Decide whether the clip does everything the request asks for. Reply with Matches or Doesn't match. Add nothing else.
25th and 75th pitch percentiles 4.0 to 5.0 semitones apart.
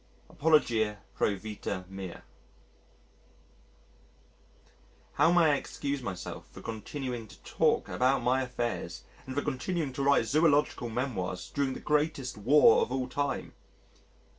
Matches